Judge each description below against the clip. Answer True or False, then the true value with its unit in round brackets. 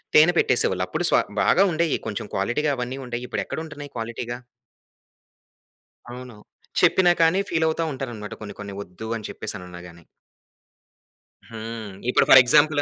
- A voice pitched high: False (120 Hz)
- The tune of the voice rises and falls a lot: True (5.8 semitones)